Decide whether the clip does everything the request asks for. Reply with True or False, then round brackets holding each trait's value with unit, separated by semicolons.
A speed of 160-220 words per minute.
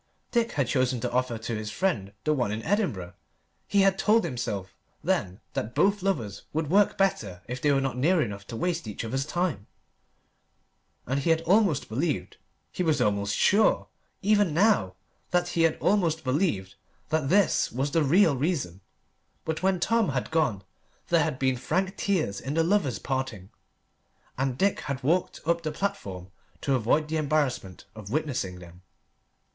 True (170 wpm)